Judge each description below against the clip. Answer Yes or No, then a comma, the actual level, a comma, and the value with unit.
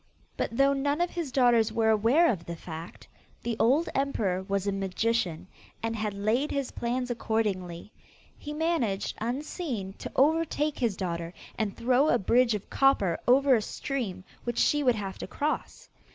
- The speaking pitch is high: Yes, high, 230 Hz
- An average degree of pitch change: No, wide, 5.8 semitones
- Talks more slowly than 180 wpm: Yes, average, 165 wpm